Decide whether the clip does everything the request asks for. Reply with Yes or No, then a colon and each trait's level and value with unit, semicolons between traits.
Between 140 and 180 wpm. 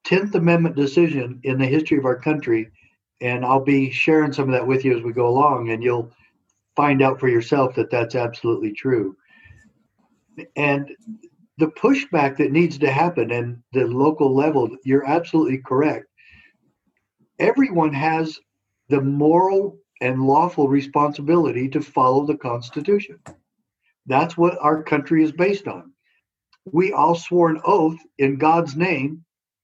Yes: average, 145 wpm